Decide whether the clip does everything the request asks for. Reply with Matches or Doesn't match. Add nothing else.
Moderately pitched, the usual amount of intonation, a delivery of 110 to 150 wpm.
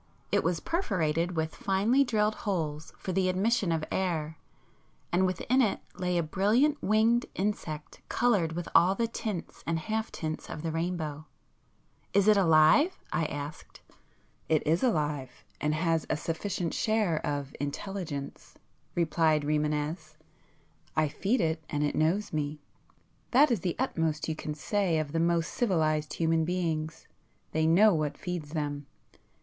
Matches